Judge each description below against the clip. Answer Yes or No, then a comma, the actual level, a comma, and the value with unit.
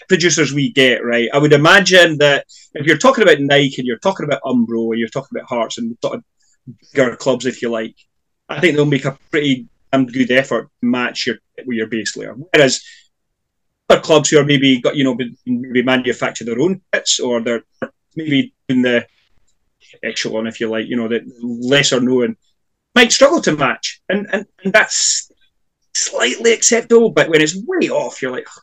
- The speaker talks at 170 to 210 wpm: Yes, average, 195 wpm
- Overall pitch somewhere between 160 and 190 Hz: No, low, 135 Hz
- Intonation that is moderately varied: No, wide, 7.0 semitones